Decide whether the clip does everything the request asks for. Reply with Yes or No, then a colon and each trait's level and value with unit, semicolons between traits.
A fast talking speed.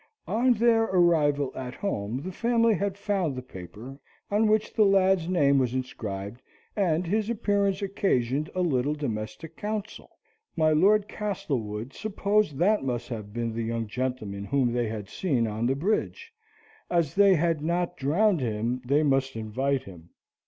No: average, 160 wpm